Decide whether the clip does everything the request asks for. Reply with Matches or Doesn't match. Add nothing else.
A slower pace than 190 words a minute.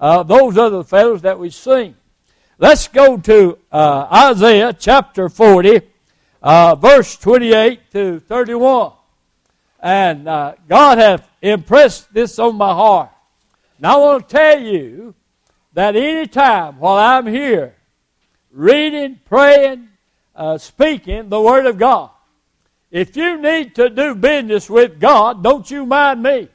Matches